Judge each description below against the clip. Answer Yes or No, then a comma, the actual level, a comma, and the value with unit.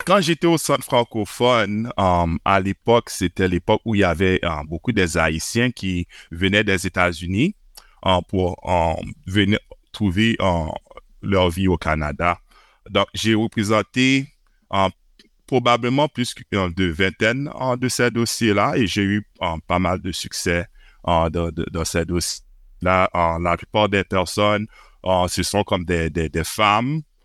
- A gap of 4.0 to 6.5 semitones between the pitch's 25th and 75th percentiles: Yes, average, 4.3 semitones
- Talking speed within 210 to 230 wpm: No, average, 165 wpm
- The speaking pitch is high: No, very low, 95 Hz